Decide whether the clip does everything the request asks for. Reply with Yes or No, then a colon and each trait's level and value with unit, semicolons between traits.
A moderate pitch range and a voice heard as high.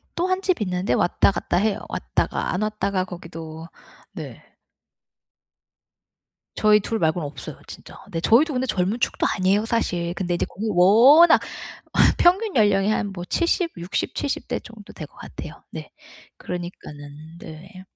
Yes: average, 4.7 semitones; high, 195 Hz